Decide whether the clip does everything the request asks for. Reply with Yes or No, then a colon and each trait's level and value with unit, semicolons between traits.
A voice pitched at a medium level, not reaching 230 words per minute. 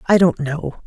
Yes: medium, 160 Hz; fast, 210 wpm